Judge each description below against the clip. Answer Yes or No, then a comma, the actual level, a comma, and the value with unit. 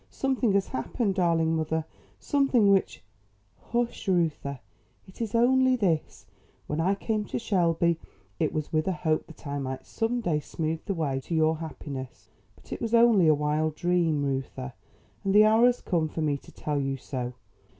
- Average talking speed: Yes, average, 180 wpm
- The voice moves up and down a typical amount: No, wide, 5.8 semitones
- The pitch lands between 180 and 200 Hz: No, medium, 165 Hz